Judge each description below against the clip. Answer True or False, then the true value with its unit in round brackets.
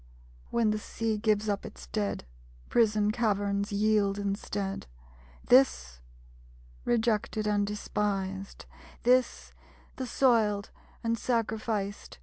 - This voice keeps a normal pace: False (100 wpm)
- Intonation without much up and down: True (2.1 semitones)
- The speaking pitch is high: True (210 Hz)